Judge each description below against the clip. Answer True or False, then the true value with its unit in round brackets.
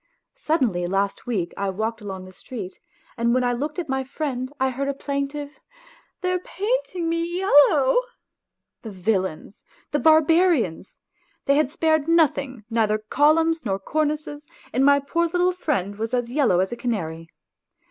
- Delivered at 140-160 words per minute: False (170 wpm)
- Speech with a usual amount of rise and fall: False (6.5 semitones)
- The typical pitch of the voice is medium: False (275 Hz)